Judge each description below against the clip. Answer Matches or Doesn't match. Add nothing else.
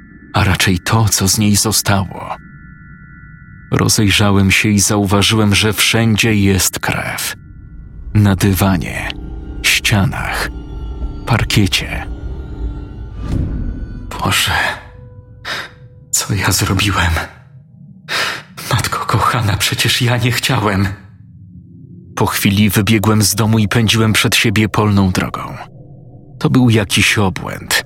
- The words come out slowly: Matches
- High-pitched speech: Doesn't match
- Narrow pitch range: Doesn't match